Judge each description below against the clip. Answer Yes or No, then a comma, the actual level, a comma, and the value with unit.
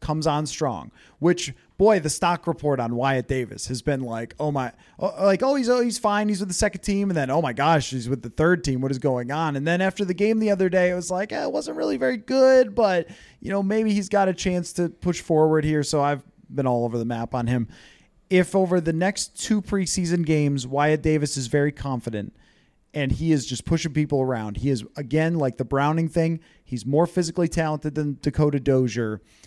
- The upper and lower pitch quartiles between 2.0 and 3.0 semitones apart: No, wide, 5.4 semitones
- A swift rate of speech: Yes, fast, 230 wpm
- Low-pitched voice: No, medium, 155 Hz